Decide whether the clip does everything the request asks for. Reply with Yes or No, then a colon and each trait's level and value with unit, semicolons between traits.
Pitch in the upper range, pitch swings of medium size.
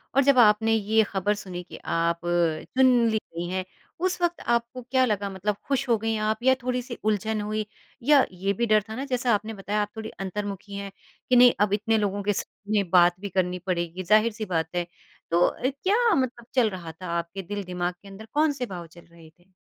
Yes: high, 210 Hz; average, 4.2 semitones